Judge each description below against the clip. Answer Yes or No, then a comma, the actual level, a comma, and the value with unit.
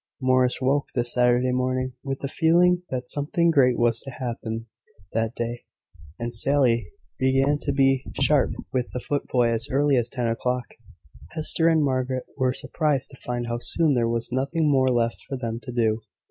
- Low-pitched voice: Yes, low, 130 Hz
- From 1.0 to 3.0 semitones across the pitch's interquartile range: Yes, narrow, 2.6 semitones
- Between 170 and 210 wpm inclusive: Yes, average, 175 wpm